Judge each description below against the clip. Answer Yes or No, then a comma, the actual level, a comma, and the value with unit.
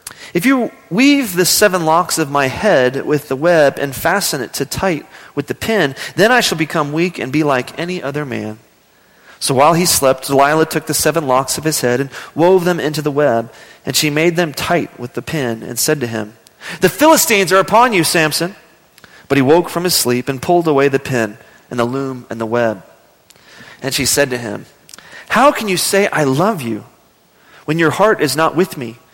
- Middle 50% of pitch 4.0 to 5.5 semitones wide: Yes, average, 5.0 semitones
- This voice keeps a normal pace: No, fast, 210 wpm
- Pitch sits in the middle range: Yes, medium, 155 Hz